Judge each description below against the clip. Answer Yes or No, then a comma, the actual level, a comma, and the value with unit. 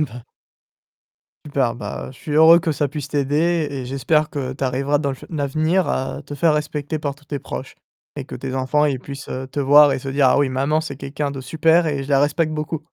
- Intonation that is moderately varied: No, narrow, 2.2 semitones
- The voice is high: No, medium, 145 Hz